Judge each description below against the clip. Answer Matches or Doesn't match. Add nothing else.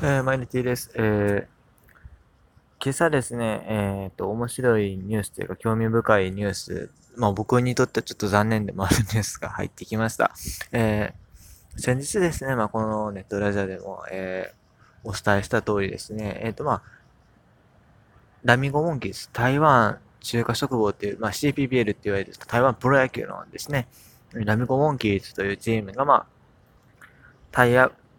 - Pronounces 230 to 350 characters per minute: Doesn't match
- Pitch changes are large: Doesn't match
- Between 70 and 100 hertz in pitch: Doesn't match